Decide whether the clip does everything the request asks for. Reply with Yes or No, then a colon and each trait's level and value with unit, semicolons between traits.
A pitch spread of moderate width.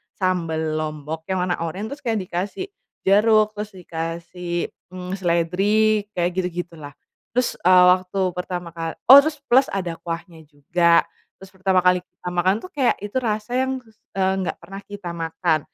Yes: average, 3.6 semitones